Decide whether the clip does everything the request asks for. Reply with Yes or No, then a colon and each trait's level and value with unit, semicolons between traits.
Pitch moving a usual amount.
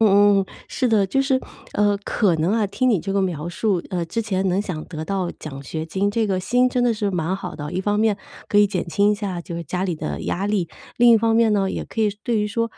Yes: average, 3.4 semitones